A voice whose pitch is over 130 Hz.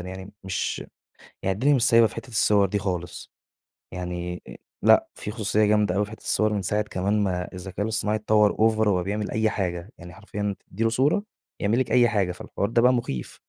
No: low, 105 Hz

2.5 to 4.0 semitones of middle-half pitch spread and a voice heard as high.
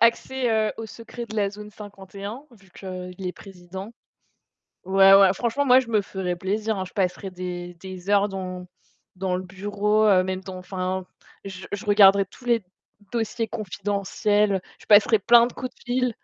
Yes: average, 2.8 semitones; high, 200 Hz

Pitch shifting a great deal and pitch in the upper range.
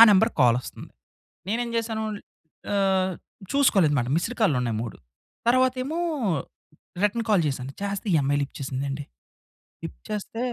Yes: wide, 8.5 semitones; high, 195 Hz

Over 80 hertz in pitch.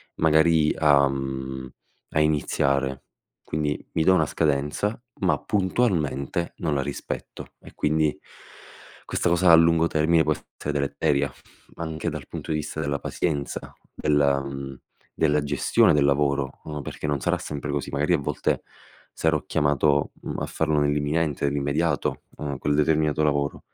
No: very low, 75 Hz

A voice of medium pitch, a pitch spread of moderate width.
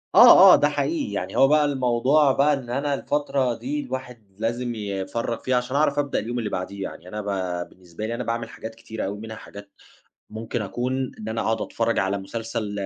No: low, 115 Hz; average, 3.9 semitones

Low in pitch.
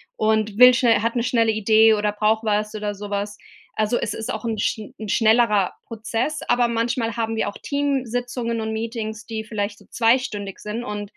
No: high, 220 Hz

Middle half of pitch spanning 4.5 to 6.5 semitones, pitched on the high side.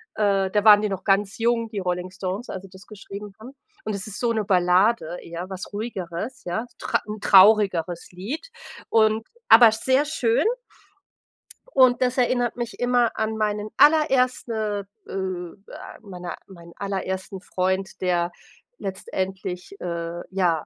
No: average, 3.5 semitones; high, 200 Hz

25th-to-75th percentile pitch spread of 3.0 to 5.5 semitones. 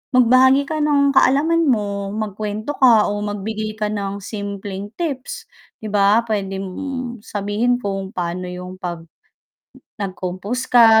Yes: average, 4.2 semitones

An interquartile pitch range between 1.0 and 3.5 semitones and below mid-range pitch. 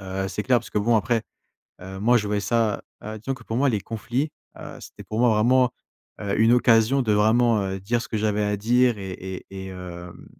Yes: average, 3.2 semitones; low, 110 Hz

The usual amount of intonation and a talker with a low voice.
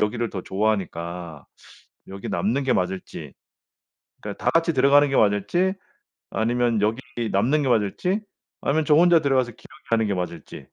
No: wide, 6.2 semitones; low, 115 Hz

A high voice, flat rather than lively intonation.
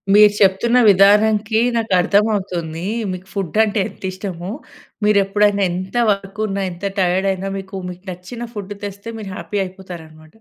Yes: high, 195 Hz; narrow, 2.2 semitones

